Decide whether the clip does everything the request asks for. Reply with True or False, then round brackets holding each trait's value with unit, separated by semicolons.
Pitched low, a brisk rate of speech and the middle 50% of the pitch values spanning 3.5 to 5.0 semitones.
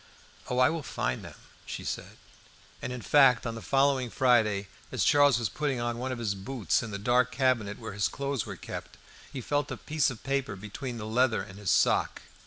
True (125 Hz; 210 wpm; 3.8 semitones)